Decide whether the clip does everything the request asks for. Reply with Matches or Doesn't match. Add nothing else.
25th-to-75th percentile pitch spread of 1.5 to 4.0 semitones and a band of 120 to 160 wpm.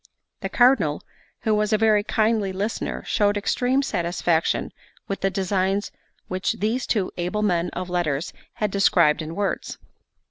Matches